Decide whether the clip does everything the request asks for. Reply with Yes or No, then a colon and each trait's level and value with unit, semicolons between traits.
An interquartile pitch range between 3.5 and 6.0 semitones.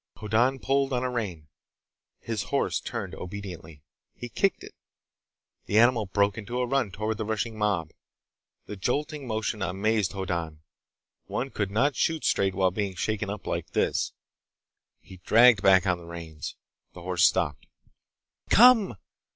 Yes: average, 4.7 semitones